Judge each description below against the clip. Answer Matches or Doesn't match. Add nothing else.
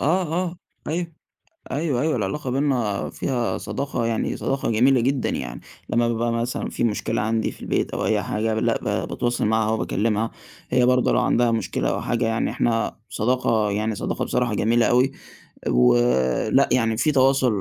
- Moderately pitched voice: Doesn't match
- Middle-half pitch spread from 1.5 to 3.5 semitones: Matches